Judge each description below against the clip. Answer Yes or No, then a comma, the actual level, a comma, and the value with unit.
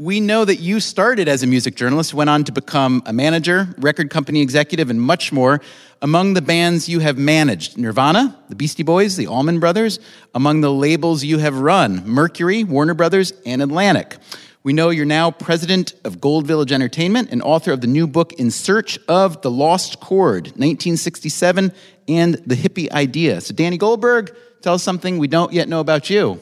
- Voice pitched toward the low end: No, medium, 165 Hz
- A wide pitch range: No, average, 3.9 semitones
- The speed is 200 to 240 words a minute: No, average, 190 wpm